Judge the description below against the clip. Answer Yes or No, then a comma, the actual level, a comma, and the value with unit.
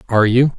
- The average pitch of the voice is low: Yes, low, 120 Hz